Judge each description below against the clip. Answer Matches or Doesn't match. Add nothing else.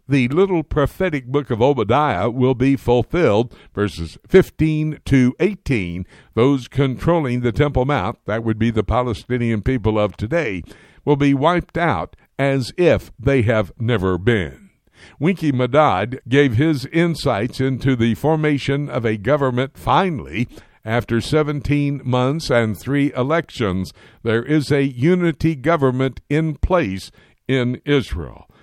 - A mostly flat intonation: Doesn't match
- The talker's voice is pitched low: Matches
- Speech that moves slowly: Matches